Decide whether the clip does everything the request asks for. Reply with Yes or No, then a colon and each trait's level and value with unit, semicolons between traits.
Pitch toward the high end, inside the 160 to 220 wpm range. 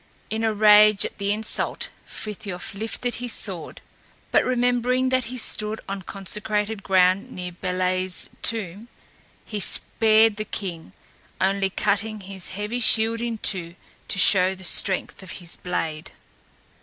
No: high, 205 Hz; average, 140 wpm